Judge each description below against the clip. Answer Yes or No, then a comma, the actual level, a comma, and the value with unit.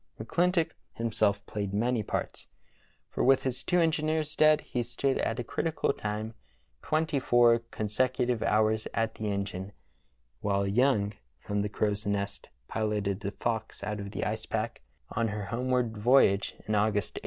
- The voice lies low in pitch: Yes, low, 110 Hz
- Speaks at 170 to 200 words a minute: No, average, 155 wpm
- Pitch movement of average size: Yes, average, 3.5 semitones